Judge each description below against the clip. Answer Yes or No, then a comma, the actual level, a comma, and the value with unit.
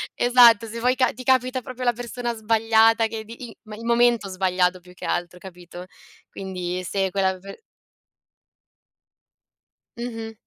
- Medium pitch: No, high, 225 Hz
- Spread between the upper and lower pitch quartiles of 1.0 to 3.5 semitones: No, average, 4.2 semitones